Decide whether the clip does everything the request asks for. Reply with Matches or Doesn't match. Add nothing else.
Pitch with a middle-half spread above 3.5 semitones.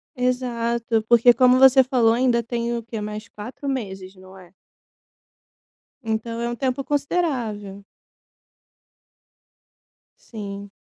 Doesn't match